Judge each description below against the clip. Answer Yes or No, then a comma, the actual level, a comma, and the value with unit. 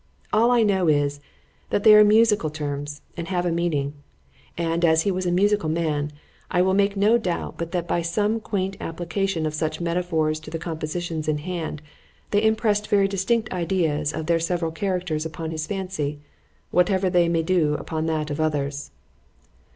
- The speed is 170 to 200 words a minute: Yes, average, 175 wpm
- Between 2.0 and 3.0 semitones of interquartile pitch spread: No, average, 3.7 semitones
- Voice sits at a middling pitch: Yes, medium, 170 Hz